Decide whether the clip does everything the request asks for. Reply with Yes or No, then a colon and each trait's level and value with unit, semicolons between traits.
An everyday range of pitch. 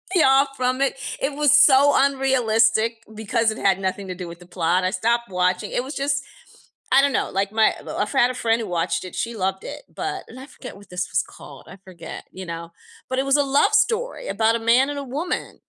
No: wide, 6.2 semitones